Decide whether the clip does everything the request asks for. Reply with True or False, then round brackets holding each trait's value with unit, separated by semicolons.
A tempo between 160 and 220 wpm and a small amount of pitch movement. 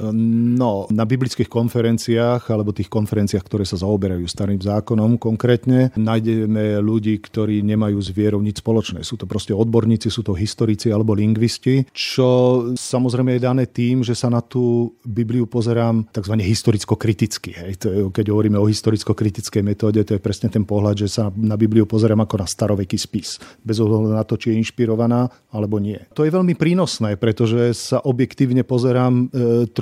True (165 wpm; 2.1 semitones)